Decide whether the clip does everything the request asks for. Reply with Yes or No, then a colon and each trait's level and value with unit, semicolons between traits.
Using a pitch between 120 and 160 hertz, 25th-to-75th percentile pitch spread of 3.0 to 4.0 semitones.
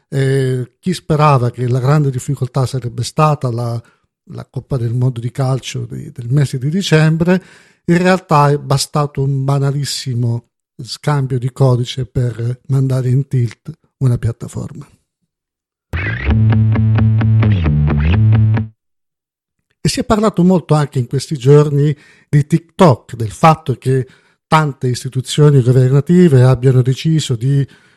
Yes: low, 135 Hz; average, 3.3 semitones